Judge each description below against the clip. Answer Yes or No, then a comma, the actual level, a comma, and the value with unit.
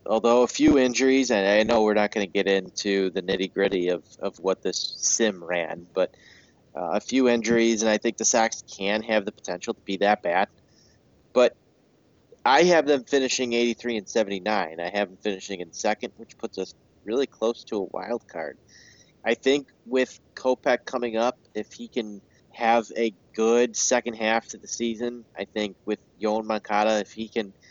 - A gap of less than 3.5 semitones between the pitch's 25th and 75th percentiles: Yes, average, 2.8 semitones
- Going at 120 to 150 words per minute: No, average, 195 wpm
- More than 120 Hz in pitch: No, low, 110 Hz